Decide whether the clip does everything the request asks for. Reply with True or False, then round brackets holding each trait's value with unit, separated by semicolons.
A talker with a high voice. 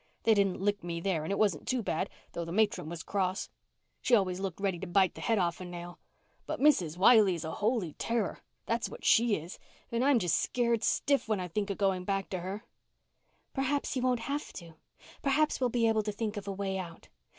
True (200 Hz)